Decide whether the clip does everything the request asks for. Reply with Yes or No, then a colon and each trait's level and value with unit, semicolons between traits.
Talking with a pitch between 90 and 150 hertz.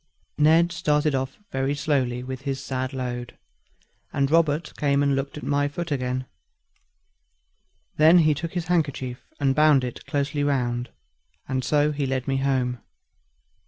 Yes: medium, 140 Hz